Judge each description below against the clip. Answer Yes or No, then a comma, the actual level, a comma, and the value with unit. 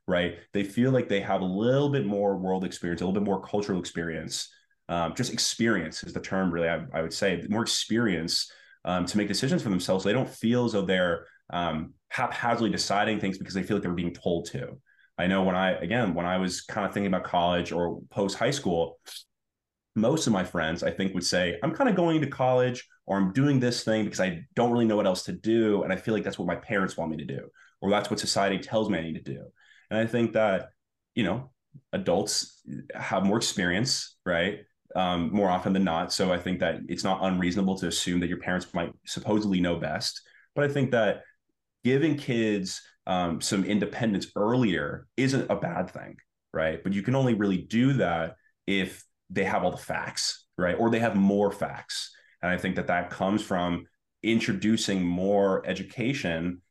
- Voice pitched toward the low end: Yes, very low, 95 Hz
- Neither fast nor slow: No, fast, 210 wpm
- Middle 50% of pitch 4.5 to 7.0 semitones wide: No, average, 4.0 semitones